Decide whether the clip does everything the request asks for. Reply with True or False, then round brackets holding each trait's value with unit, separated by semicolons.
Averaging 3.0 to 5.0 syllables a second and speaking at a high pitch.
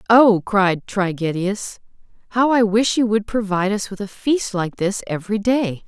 True (4.6 syllables/s; 205 Hz)